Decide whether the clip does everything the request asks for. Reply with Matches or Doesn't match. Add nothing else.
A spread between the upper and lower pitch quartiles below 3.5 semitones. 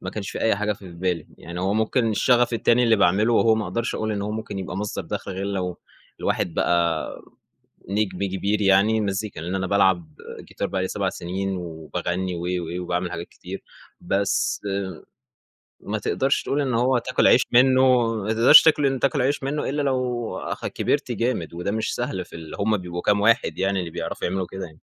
Doesn't match